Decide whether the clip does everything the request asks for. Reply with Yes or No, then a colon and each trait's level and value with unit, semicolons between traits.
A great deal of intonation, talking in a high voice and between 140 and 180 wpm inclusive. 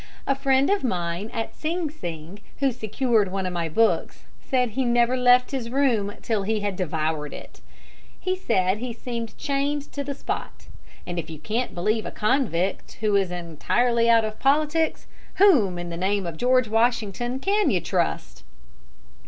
Yes: wide, 6.1 semitones; high, 225 Hz; average, 170 wpm